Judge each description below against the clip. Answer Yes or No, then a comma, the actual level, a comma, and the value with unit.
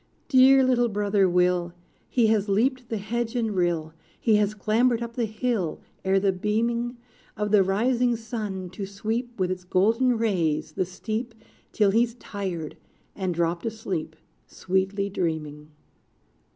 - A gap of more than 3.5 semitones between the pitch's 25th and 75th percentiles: Yes, average, 4.1 semitones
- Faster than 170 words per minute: No, average, 145 wpm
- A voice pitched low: No, high, 210 Hz